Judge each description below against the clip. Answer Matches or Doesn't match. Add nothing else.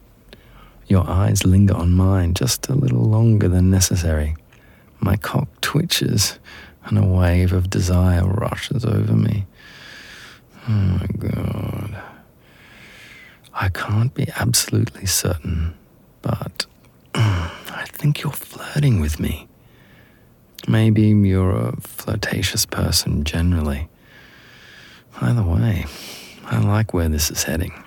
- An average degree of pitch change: Matches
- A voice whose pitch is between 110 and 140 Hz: Doesn't match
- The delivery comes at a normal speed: Doesn't match